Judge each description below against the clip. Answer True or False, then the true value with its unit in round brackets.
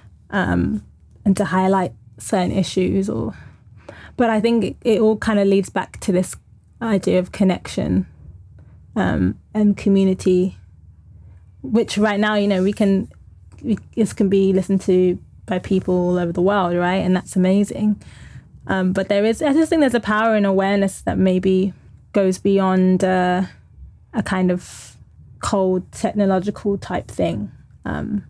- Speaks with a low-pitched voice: False (190 Hz)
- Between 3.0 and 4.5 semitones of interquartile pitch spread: False (2.4 semitones)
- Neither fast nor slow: True (155 wpm)